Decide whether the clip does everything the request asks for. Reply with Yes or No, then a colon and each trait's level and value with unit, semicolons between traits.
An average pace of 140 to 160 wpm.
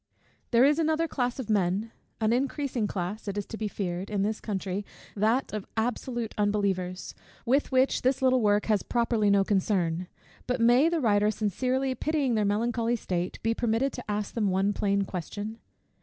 No: average, 180 wpm